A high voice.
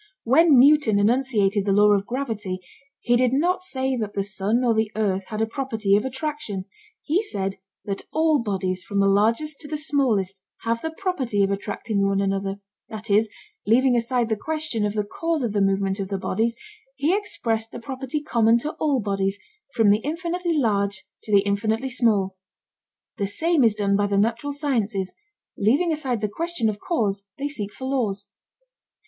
Yes: high, 225 Hz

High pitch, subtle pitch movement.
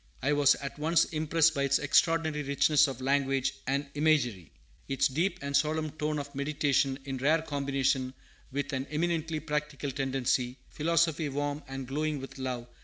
No: medium, 145 Hz; narrow, 2.3 semitones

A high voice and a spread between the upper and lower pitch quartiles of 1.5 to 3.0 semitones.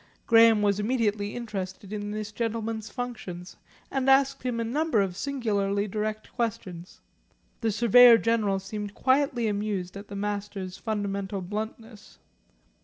Yes: high, 215 Hz; narrow, 2.5 semitones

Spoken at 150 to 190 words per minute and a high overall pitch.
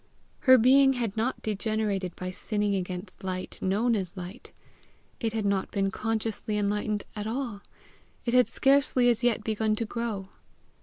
Yes: average, 155 wpm; high, 215 Hz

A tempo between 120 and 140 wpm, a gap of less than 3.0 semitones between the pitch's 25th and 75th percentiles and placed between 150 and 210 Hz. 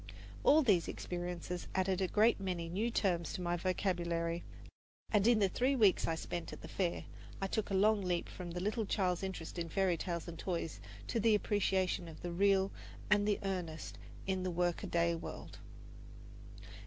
No: average, 180 wpm; narrow, 2.6 semitones; medium, 185 Hz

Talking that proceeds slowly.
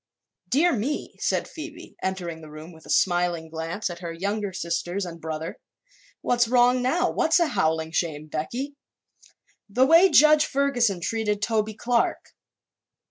No: average, 145 wpm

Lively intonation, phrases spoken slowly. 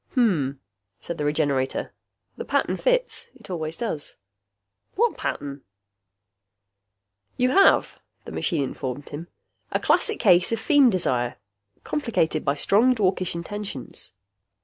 Yes: wide, 8.1 semitones; slow, 120 wpm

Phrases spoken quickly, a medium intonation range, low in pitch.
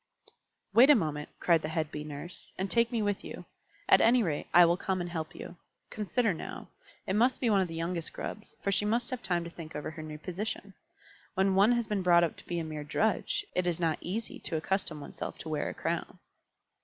No: fast, 230 wpm; average, 4.7 semitones; medium, 180 Hz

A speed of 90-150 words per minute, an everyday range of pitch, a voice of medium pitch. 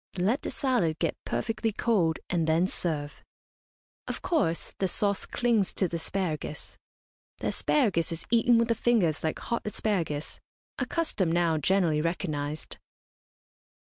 No: average, 140 wpm; wide, 5.8 semitones; medium, 180 Hz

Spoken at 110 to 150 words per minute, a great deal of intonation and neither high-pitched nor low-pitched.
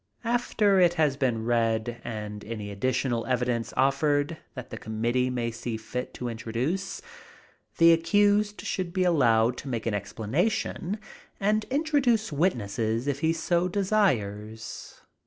No: slow, 135 wpm; wide, 8.0 semitones; low, 130 Hz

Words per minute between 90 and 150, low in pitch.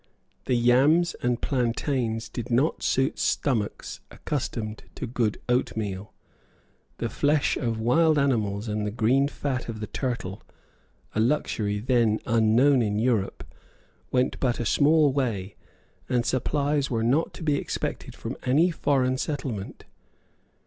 Yes: slow, 135 wpm; low, 125 Hz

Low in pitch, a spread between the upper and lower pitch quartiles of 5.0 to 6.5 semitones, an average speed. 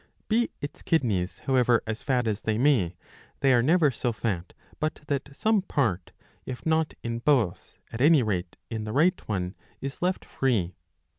Yes: low, 125 Hz; wide, 5.6 semitones; average, 170 wpm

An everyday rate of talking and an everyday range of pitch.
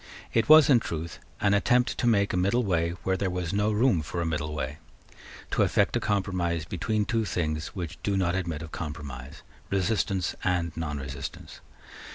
Yes: average, 180 wpm; average, 4.2 semitones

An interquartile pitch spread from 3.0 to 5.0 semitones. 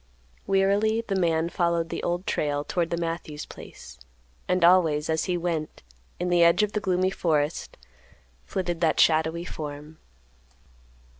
No: narrow, 2.4 semitones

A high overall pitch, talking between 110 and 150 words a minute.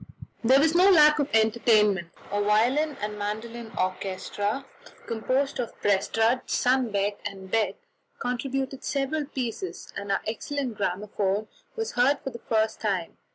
Yes: high, 225 Hz; slow, 135 wpm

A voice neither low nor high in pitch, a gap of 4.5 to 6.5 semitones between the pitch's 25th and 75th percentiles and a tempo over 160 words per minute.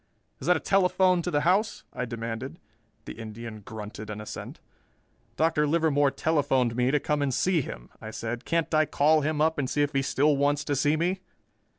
Yes: medium, 145 Hz; average, 4.8 semitones; average, 200 wpm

